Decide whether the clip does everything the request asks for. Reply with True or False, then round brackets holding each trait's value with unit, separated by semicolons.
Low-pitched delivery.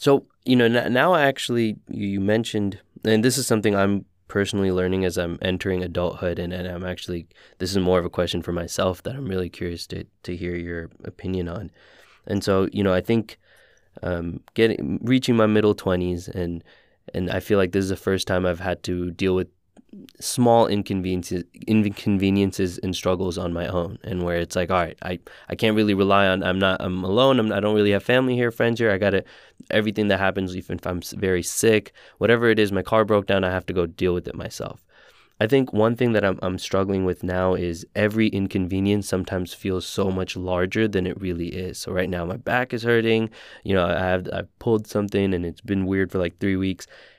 True (95 Hz)